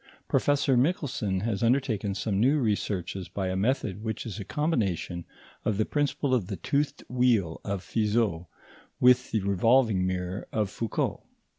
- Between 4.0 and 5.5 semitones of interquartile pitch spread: Yes, average, 4.7 semitones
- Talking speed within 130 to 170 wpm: Yes, average, 150 wpm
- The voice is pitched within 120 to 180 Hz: No, low, 110 Hz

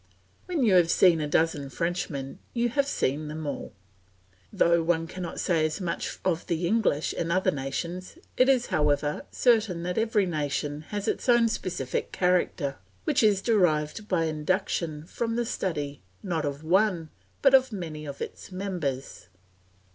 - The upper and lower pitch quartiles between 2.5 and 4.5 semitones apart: No, average, 5.2 semitones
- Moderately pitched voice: Yes, medium, 170 Hz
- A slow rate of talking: No, average, 155 wpm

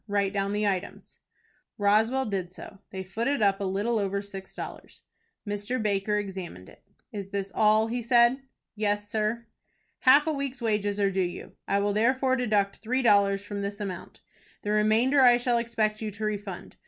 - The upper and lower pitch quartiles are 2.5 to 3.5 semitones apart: Yes, average, 2.8 semitones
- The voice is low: No, high, 210 Hz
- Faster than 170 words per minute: Yes, average, 180 wpm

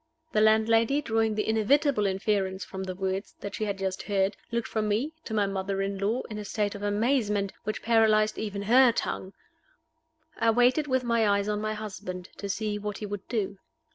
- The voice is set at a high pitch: Yes, high, 210 Hz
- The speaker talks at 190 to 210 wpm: Yes, average, 200 wpm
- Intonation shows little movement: Yes, narrow, 2.1 semitones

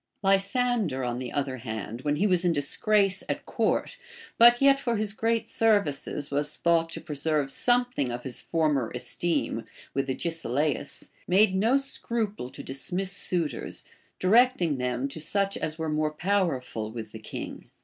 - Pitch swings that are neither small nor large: No, wide, 6.9 semitones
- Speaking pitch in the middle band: Yes, medium, 165 Hz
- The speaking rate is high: No, average, 155 wpm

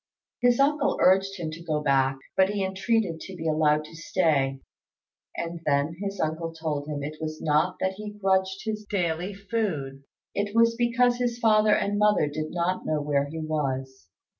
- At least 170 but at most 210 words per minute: Yes, average, 180 wpm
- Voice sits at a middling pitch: Yes, medium, 170 Hz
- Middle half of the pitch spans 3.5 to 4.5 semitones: No, average, 5.1 semitones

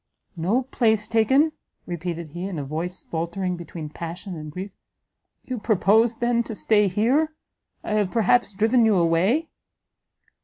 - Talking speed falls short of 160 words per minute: Yes, average, 145 wpm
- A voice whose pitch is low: No, high, 200 Hz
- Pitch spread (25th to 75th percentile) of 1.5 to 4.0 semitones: No, average, 5.2 semitones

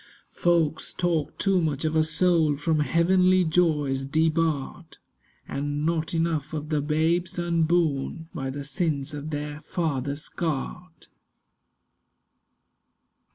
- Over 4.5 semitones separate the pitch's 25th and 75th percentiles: No, narrow, 2.4 semitones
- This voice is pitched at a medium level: Yes, medium, 160 Hz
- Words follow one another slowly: Yes, slow, 110 wpm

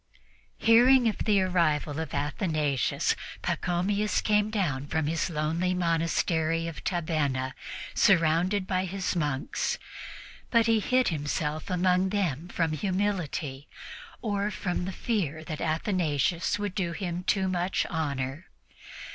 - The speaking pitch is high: No, medium, 175 Hz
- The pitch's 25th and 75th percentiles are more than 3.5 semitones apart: Yes, average, 3.9 semitones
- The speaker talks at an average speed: No, slow, 120 wpm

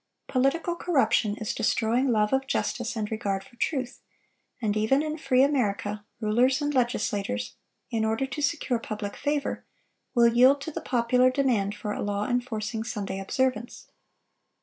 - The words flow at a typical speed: Yes, average, 150 wpm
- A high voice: Yes, high, 240 Hz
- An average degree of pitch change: Yes, average, 3.9 semitones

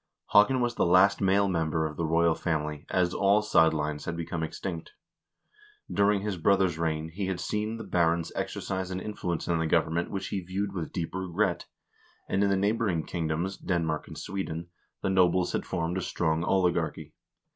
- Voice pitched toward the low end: Yes, very low, 90 Hz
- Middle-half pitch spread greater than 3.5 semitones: No, average, 3.0 semitones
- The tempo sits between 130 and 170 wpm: No, average, 180 wpm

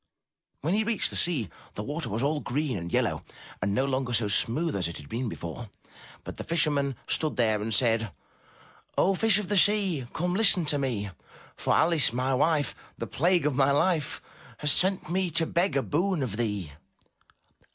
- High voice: No, medium, 140 Hz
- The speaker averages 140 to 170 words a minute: No, average, 190 wpm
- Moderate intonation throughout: No, wide, 6.8 semitones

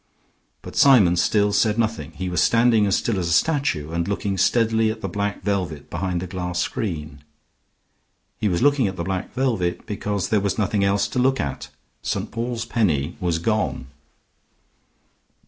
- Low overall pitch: Yes, low, 100 Hz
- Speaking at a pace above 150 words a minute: Yes, average, 170 wpm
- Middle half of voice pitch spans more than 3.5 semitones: Yes, average, 4.3 semitones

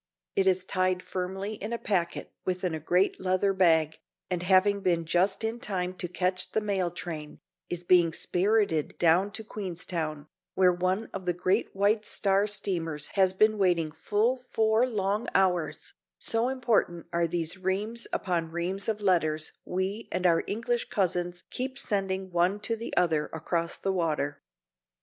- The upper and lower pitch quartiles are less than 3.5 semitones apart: Yes, average, 2.9 semitones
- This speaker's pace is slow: No, average, 160 wpm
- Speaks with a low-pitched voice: No, medium, 185 Hz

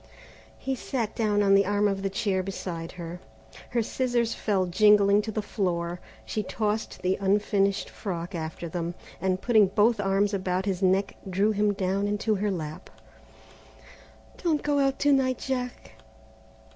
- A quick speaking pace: No, average, 160 wpm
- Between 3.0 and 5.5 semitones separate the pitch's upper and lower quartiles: No, narrow, 2.6 semitones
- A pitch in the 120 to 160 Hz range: No, high, 200 Hz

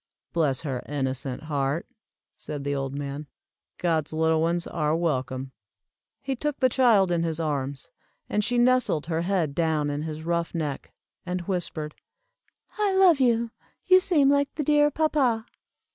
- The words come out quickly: No, average, 155 wpm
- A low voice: No, medium, 165 Hz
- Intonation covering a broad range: Yes, wide, 8.7 semitones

